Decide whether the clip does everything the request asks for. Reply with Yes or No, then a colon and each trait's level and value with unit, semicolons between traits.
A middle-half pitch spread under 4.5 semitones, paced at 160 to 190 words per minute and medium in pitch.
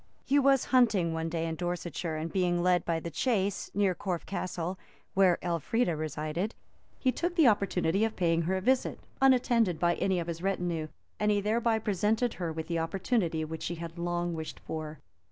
Yes: average, 4.1 semitones; average, 185 wpm; medium, 180 Hz